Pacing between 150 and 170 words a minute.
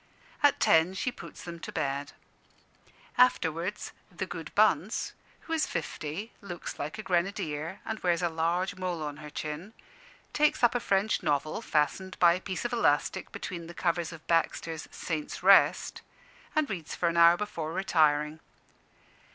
Yes: average, 160 wpm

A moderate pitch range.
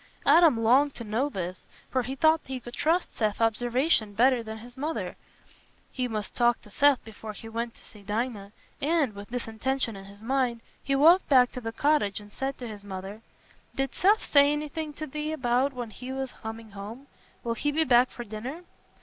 Yes: average, 4.1 semitones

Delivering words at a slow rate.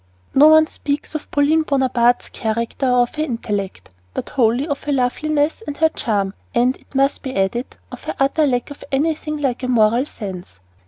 No: average, 180 wpm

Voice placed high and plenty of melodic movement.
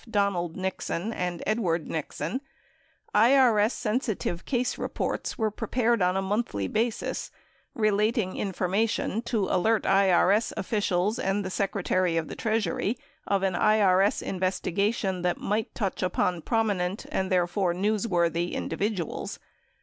No: high, 200 Hz; average, 3.2 semitones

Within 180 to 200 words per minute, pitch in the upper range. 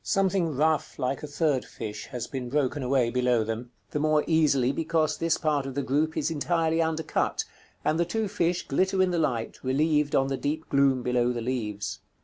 No: average, 195 wpm; medium, 145 Hz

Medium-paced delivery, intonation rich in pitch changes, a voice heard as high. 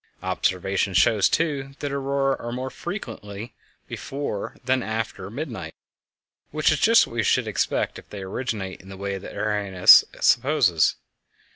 No: average, 145 wpm; wide, 5.9 semitones; low, 115 Hz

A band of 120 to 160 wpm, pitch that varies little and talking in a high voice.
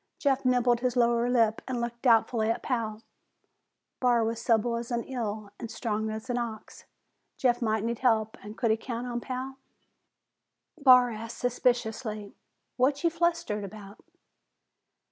Yes: average, 150 wpm; narrow, 2.3 semitones; high, 235 Hz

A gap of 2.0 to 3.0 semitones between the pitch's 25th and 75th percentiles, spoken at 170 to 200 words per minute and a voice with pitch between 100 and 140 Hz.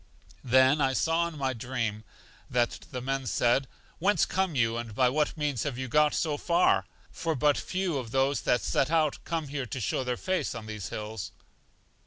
No: average, 4.1 semitones; average, 195 wpm; low, 135 Hz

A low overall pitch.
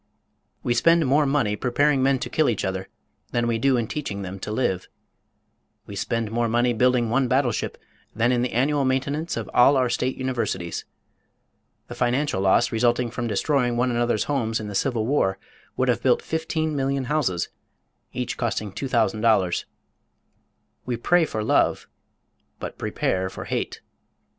Yes: low, 120 Hz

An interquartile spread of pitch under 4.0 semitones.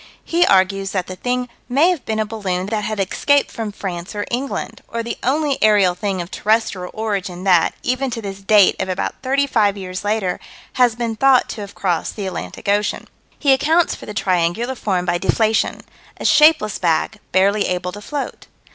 No: average, 4.6 semitones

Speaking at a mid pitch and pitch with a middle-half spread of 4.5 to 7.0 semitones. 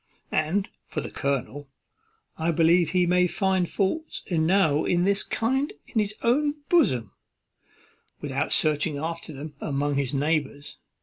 Yes: medium, 165 Hz; average, 5.1 semitones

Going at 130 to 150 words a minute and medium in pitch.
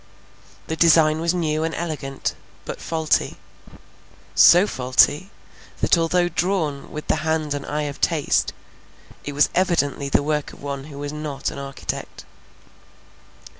Yes: average, 140 wpm; medium, 155 Hz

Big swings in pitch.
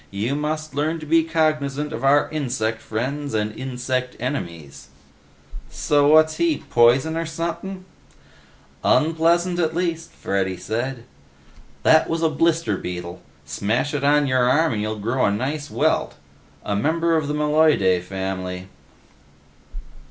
Yes: wide, 6.5 semitones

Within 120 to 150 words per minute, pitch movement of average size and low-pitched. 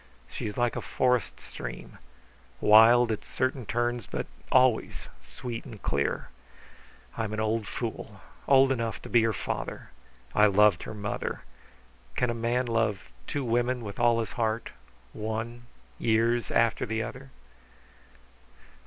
No: average, 140 wpm; narrow, 2.0 semitones; low, 115 Hz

